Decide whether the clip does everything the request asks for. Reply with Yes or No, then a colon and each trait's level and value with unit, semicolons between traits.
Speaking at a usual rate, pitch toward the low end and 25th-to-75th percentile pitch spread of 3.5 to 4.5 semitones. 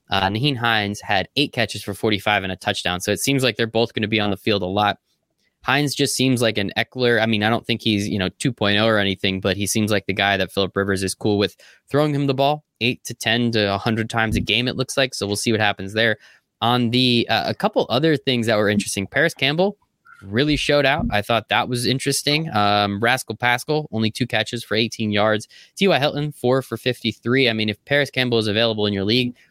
No: fast, 245 wpm; low, 115 Hz; average, 3.8 semitones